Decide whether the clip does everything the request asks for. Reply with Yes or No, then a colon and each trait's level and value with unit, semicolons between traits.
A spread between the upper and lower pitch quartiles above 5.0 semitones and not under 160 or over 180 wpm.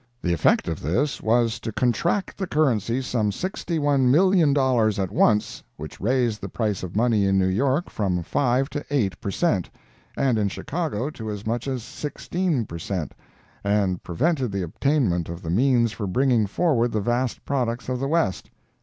Yes: wide, 5.4 semitones; average, 170 wpm